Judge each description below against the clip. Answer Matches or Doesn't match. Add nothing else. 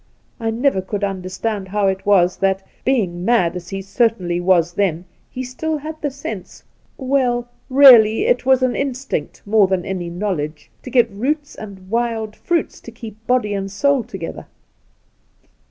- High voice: Matches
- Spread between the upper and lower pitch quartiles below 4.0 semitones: Doesn't match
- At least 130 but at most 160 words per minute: Doesn't match